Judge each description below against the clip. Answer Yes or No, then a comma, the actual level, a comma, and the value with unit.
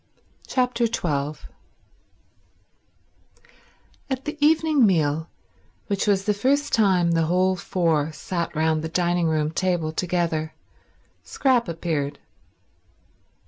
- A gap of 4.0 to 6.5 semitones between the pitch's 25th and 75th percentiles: Yes, average, 5.2 semitones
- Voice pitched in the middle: Yes, medium, 175 Hz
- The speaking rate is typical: No, slow, 100 wpm